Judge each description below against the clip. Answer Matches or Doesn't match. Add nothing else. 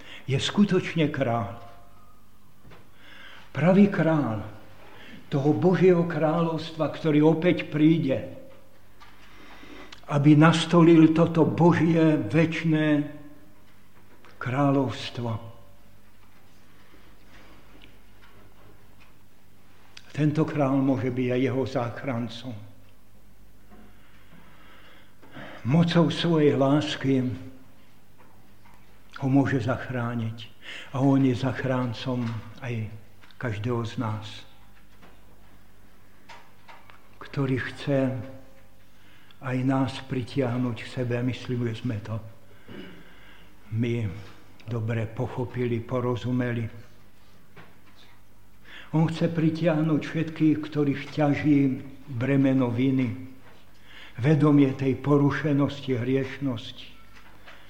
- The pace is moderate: Doesn't match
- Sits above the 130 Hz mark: Doesn't match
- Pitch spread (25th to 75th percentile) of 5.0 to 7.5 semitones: Matches